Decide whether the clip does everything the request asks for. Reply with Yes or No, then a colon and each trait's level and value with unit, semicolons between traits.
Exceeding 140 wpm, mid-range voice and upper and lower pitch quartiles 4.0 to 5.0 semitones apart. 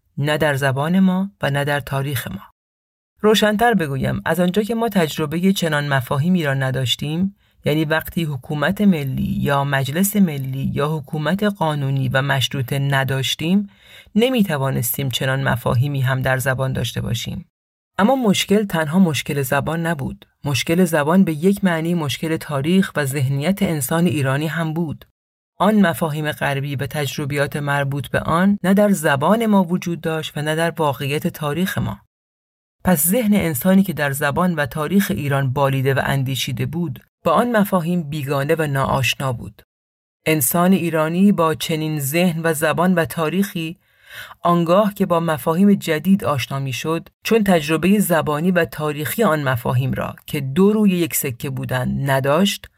Yes: average, 150 wpm; medium, 155 Hz; average, 4.7 semitones